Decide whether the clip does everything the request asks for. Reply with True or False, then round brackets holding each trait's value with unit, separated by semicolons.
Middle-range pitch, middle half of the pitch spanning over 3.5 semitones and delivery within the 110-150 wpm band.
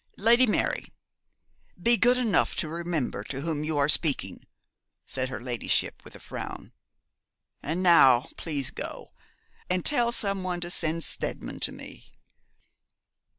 True (170 Hz; 5.6 semitones; 140 wpm)